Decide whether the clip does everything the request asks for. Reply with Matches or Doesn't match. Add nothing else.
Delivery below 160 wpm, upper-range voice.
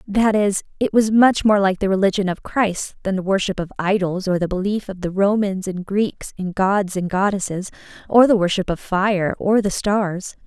Doesn't match